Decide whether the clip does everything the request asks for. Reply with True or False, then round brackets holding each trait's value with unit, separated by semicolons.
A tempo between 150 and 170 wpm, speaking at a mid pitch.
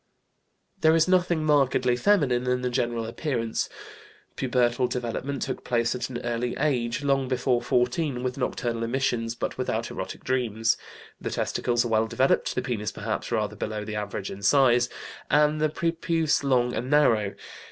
False (160 wpm; 125 Hz)